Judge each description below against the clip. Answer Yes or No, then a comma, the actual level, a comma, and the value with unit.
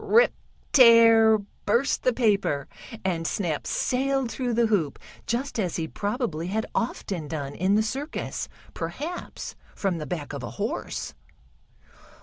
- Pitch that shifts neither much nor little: No, wide, 6.4 semitones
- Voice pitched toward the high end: Yes, high, 215 Hz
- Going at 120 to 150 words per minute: Yes, slow, 135 wpm